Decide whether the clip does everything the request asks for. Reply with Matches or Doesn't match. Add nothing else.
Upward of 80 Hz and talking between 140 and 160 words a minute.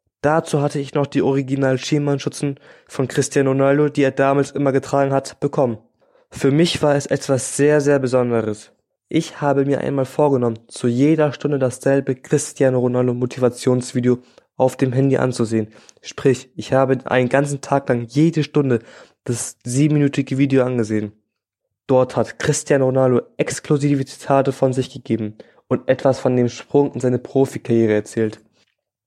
Matches